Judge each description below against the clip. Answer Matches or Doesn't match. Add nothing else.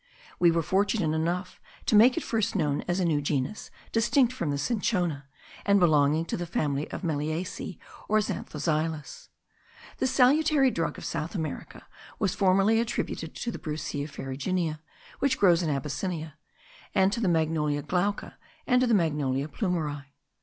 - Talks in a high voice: Doesn't match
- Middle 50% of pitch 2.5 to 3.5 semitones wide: Doesn't match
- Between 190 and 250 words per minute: Doesn't match